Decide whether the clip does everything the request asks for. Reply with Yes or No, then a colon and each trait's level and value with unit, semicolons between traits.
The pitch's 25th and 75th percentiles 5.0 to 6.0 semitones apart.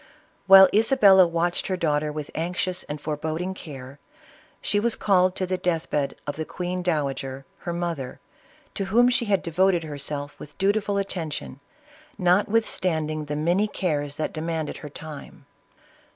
No: average, 4.1 semitones